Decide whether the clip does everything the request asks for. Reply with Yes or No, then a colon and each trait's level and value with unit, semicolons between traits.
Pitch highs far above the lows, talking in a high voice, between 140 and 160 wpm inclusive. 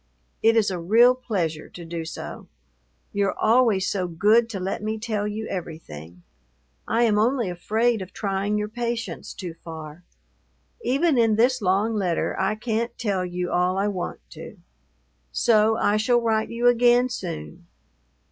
No: average, 4.3 semitones; high, 210 Hz; average, 155 wpm